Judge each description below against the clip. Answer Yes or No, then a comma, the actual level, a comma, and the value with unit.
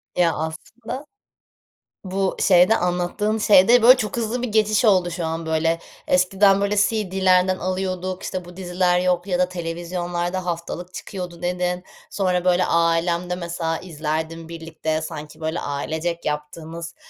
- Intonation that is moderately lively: No, narrow, 2.1 semitones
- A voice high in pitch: No, medium, 180 Hz